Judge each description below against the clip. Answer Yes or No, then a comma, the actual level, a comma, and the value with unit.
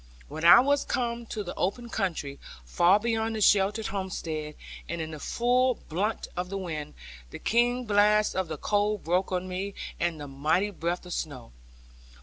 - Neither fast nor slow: Yes, average, 175 wpm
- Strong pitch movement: No, average, 4.6 semitones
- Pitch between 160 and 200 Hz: Yes, high, 190 Hz